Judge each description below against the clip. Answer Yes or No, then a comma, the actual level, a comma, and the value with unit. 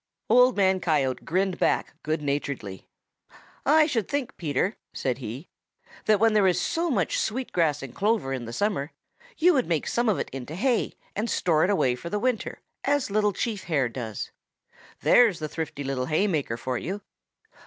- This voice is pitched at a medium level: Yes, medium, 180 Hz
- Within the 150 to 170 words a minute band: No, average, 180 wpm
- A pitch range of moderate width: No, wide, 8.0 semitones